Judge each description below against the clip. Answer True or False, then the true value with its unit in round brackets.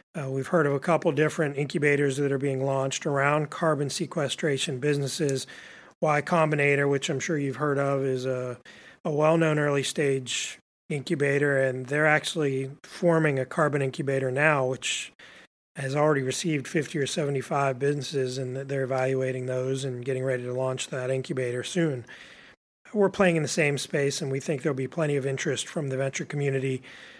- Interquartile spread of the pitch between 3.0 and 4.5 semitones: False (2.5 semitones)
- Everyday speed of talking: True (170 wpm)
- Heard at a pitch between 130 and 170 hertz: True (140 Hz)